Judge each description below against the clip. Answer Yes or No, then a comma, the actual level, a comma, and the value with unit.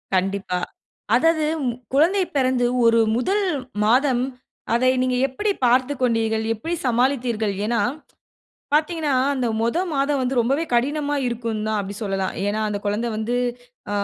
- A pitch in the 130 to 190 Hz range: No, high, 245 Hz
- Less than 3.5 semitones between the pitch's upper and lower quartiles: No, average, 4.0 semitones